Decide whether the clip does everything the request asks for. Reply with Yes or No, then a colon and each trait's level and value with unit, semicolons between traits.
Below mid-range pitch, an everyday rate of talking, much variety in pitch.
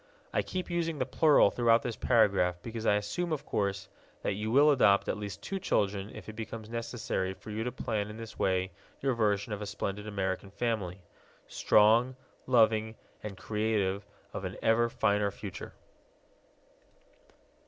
No: low, 110 Hz; average, 165 wpm; average, 2.8 semitones